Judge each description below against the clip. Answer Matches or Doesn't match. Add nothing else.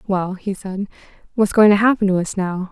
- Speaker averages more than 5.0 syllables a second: Matches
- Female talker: Matches